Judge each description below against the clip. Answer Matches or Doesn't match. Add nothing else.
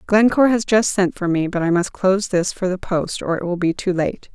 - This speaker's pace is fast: Matches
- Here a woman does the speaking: Matches